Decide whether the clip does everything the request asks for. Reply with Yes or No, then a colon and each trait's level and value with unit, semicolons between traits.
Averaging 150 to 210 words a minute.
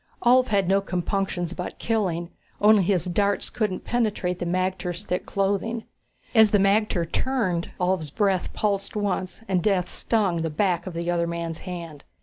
Yes: average, 160 wpm